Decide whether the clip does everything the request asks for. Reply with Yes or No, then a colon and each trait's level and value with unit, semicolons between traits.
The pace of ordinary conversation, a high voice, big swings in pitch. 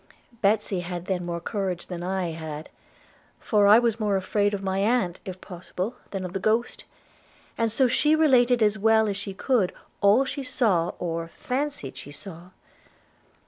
No: average, 170 wpm; high, 200 Hz; average, 4.3 semitones